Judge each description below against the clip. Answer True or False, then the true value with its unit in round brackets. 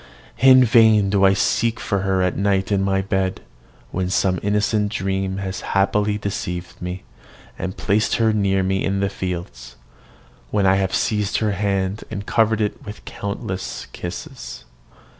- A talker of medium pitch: False (100 Hz)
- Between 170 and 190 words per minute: False (160 wpm)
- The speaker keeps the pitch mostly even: True (1.7 semitones)